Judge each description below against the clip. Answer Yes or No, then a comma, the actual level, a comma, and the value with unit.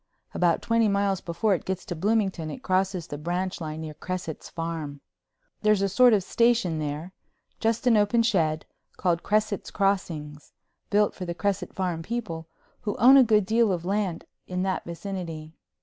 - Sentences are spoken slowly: No, average, 165 wpm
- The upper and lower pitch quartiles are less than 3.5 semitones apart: No, average, 4.2 semitones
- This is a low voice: No, medium, 185 Hz